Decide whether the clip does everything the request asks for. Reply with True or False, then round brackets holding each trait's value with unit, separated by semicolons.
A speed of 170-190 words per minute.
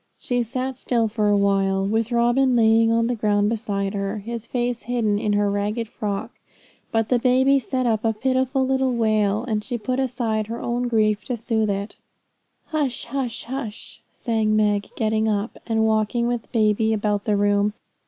True (175 wpm)